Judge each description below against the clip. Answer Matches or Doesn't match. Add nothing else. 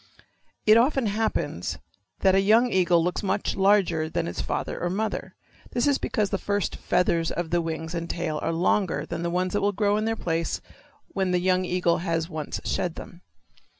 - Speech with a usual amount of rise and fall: Matches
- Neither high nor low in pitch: Matches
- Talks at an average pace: Matches